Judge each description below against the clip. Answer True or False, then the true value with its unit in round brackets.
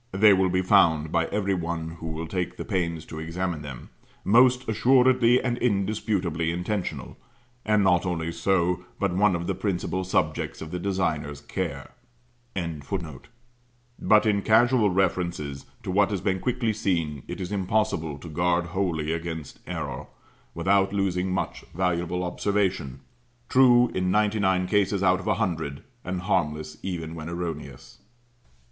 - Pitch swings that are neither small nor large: True (3.6 semitones)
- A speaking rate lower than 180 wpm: True (150 wpm)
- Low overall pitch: True (90 Hz)